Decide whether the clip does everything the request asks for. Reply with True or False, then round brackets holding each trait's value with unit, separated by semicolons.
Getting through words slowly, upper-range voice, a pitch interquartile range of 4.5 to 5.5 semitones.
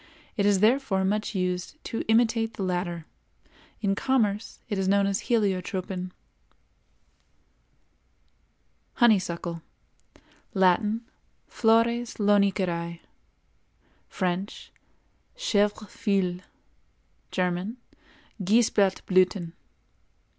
False (70 wpm; 200 Hz; 3.4 semitones)